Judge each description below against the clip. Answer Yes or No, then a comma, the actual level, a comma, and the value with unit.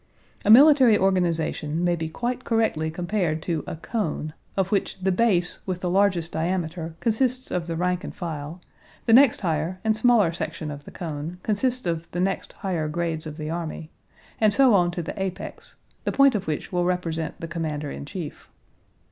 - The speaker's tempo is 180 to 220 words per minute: Yes, average, 185 wpm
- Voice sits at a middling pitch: Yes, medium, 175 Hz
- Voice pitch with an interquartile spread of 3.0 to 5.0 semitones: Yes, average, 4.1 semitones